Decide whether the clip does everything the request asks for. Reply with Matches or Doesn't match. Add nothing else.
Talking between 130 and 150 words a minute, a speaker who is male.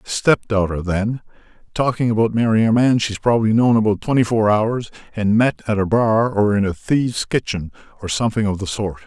Doesn't match